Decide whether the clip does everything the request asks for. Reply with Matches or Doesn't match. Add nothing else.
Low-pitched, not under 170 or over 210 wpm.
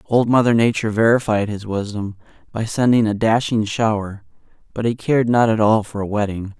Matches